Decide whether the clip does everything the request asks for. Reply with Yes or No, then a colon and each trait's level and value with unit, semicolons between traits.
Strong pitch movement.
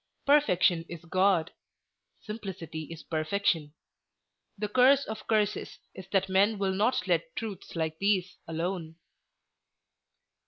No: average, 4.1 semitones